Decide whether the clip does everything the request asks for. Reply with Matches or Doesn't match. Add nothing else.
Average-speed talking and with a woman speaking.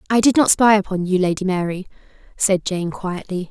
Matches